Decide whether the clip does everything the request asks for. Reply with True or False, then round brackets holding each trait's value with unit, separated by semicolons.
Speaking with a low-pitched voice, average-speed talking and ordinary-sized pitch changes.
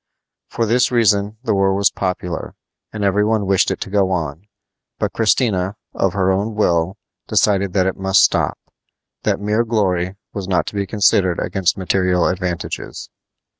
False (95 Hz; 165 wpm; 2.1 semitones)